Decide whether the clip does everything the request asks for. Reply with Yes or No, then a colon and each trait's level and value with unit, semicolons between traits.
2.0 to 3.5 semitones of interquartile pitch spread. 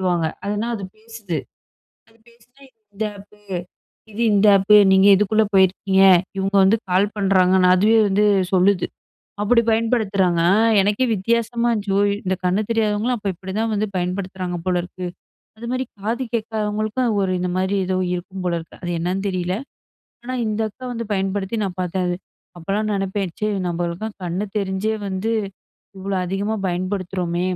Yes: average, 2.7 semitones